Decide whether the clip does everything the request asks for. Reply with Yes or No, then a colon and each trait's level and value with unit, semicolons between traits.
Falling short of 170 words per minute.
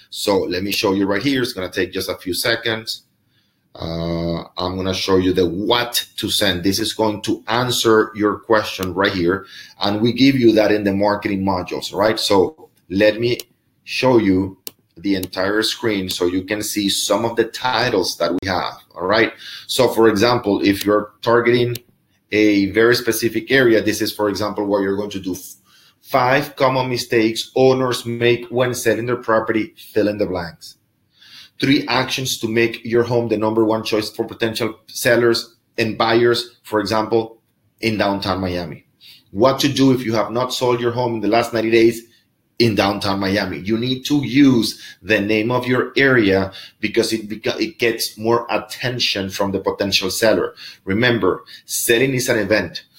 No: average, 180 wpm